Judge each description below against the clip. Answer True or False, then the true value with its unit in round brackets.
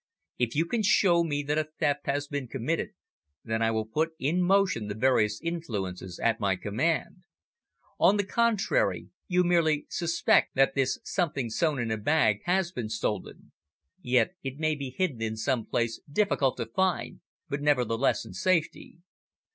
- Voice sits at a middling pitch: True (145 Hz)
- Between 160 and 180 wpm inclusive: True (165 wpm)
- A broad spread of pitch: True (6.8 semitones)